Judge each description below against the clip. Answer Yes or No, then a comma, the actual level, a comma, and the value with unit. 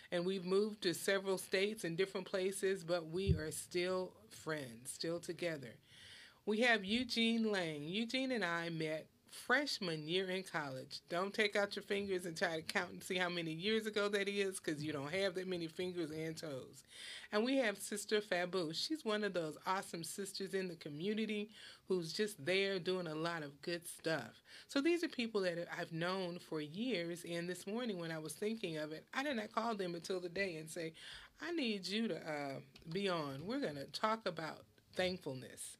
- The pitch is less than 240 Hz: Yes, medium, 185 Hz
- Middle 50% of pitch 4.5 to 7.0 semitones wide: No, average, 3.8 semitones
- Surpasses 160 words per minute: Yes, average, 200 wpm